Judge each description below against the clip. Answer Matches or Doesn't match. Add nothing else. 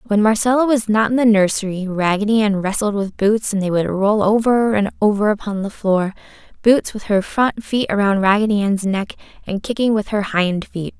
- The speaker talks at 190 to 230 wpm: Matches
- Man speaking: Doesn't match